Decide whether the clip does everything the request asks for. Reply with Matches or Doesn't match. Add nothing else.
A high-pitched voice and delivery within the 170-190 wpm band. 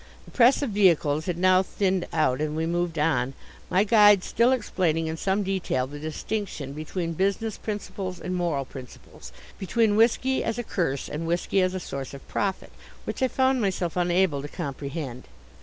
Doesn't match